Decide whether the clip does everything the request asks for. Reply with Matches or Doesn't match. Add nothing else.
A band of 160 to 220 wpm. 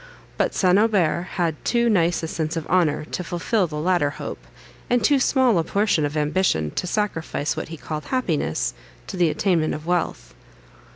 Matches